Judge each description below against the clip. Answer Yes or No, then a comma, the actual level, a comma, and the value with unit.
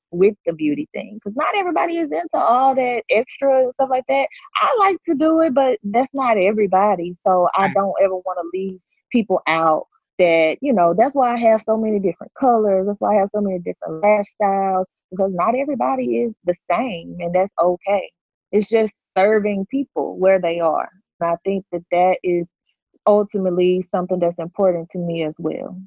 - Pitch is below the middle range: No, high, 195 Hz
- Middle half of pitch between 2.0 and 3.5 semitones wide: No, average, 4.5 semitones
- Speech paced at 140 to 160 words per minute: No, average, 195 wpm